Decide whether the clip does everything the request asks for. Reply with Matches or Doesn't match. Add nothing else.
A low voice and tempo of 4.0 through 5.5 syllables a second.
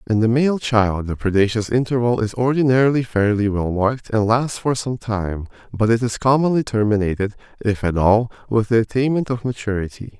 Matches